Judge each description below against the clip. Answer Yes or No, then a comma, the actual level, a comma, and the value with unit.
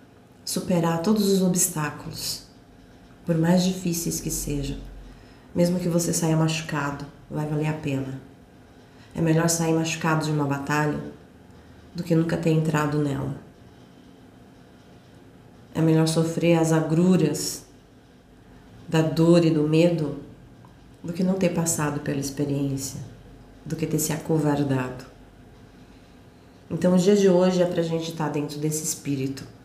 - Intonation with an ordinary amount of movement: Yes, average, 3.0 semitones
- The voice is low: No, medium, 155 Hz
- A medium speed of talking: Yes, average, 135 wpm